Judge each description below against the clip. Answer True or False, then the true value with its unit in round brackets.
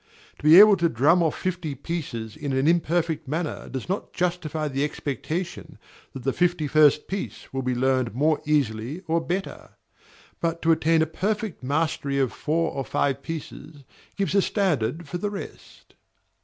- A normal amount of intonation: True (3.9 semitones)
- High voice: False (155 Hz)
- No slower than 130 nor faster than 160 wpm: False (170 wpm)